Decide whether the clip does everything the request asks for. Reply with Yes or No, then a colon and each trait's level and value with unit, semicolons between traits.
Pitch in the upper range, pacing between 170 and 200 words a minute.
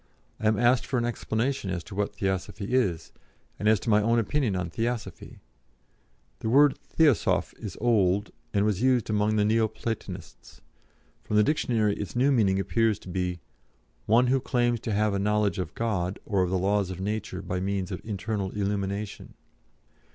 No: low, 105 Hz; average, 180 wpm